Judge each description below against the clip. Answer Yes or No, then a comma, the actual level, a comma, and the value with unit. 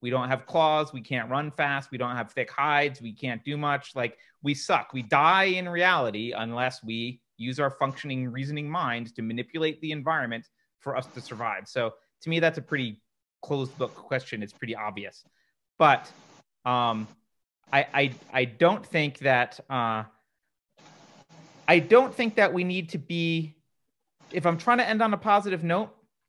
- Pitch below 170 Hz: Yes, medium, 140 Hz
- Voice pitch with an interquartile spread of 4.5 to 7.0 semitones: Yes, average, 5.2 semitones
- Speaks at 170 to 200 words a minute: Yes, average, 175 wpm